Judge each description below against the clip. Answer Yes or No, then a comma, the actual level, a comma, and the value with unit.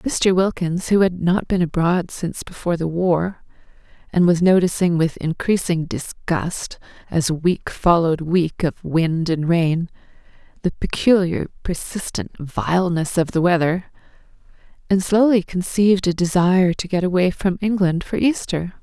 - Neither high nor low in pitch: Yes, medium, 175 Hz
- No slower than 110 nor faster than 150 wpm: Yes, average, 140 wpm